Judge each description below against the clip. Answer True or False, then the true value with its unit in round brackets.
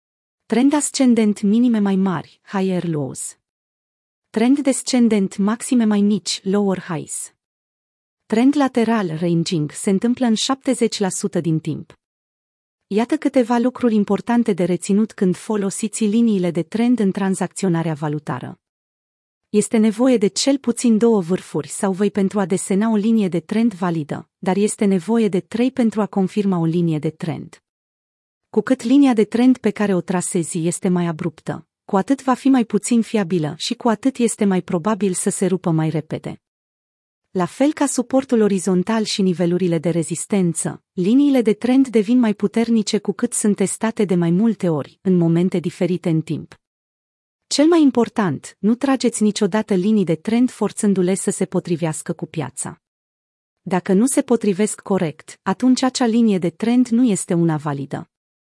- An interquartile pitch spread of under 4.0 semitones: False (4.4 semitones)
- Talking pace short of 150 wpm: False (155 wpm)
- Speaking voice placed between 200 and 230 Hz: True (205 Hz)